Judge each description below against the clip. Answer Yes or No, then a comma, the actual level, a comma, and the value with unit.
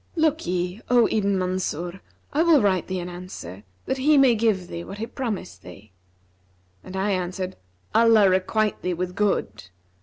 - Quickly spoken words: No, average, 160 wpm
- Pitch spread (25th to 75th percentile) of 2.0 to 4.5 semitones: Yes, average, 4.0 semitones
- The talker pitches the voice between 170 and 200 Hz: Yes, high, 190 Hz